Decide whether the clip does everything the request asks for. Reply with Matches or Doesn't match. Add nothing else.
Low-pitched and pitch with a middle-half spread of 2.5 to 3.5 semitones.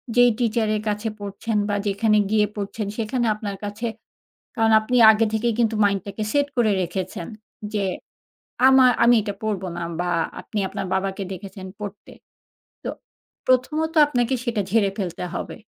Doesn't match